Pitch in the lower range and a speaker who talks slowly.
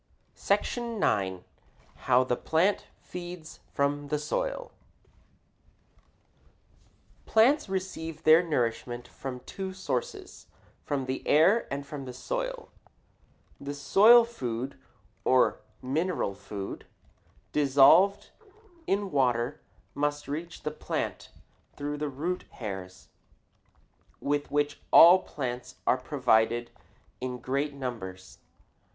No: medium, 145 Hz; slow, 100 wpm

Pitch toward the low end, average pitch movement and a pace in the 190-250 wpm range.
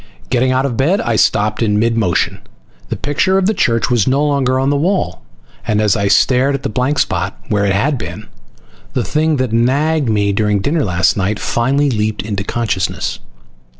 Yes: low, 120 Hz; average, 5.0 semitones; average, 200 wpm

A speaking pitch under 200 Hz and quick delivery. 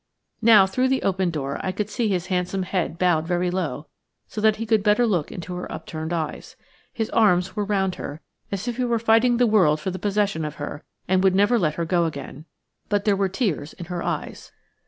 Yes: high, 190 Hz; fast, 220 wpm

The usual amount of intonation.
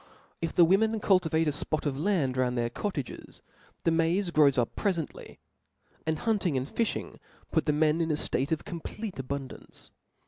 Yes: average, 4.8 semitones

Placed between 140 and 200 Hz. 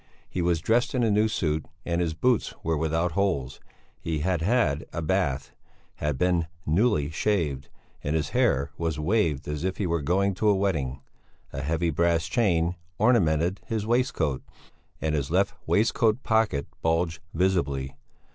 No: very low, 85 Hz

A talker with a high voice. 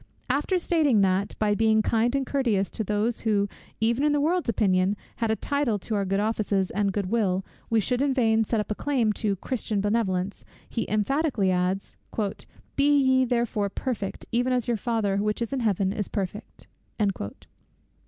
Yes: high, 220 Hz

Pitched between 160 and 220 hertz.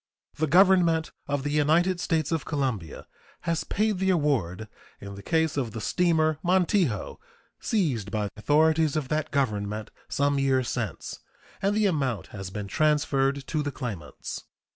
No: medium, 145 Hz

